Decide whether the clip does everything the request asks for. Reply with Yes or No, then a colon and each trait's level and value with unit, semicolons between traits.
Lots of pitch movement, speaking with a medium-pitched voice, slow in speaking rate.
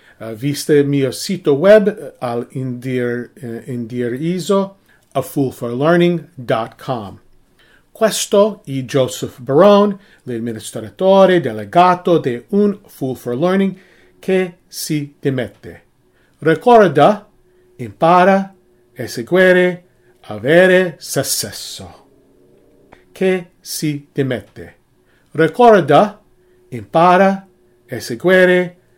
Yes: wide, 7.2 semitones; medium, 145 Hz; slow, 75 wpm